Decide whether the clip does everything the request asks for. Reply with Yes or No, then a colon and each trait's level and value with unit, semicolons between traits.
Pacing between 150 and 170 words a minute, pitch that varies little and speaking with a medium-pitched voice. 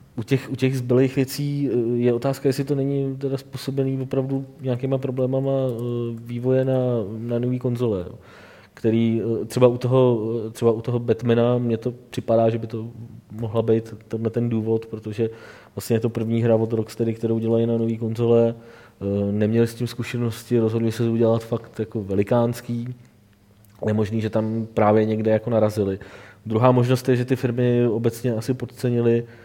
No: average, 165 wpm; narrow, 1.8 semitones; low, 115 Hz